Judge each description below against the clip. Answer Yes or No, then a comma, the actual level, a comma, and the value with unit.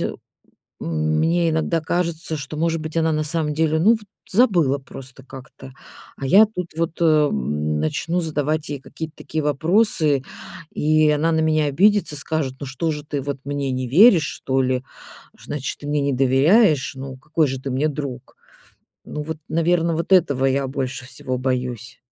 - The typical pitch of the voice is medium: Yes, medium, 150 Hz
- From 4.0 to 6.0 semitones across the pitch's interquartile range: No, average, 3.5 semitones